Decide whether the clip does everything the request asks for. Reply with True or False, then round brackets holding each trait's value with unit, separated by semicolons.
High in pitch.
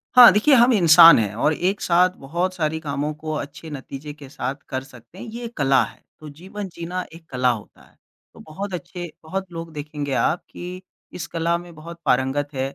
False (160 Hz)